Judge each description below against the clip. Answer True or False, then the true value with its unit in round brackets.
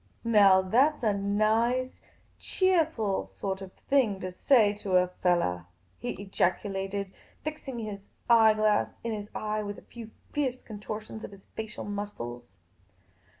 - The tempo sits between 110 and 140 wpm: False (150 wpm)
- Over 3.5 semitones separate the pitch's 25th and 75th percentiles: False (3.2 semitones)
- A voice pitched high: True (210 Hz)